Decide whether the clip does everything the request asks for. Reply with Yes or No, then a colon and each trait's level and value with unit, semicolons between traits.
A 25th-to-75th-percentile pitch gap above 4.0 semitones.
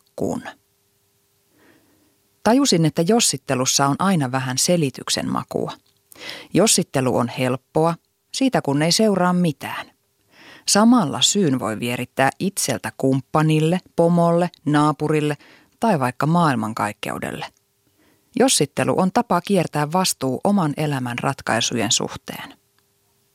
Yes: wide, 5.5 semitones